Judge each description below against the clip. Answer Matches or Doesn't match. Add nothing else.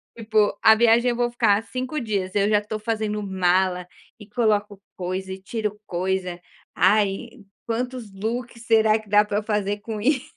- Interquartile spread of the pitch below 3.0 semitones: Matches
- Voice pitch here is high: Matches